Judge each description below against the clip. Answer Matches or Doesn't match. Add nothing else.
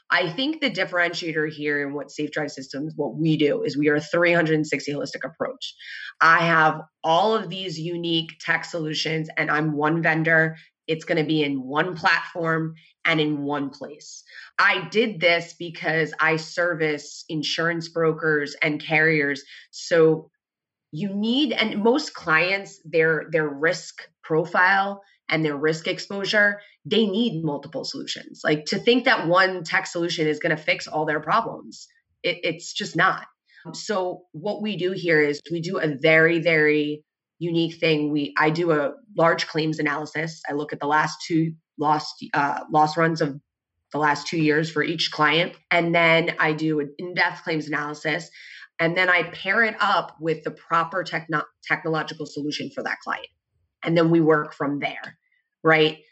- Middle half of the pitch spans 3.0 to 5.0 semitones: Doesn't match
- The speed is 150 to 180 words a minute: Matches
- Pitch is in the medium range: Matches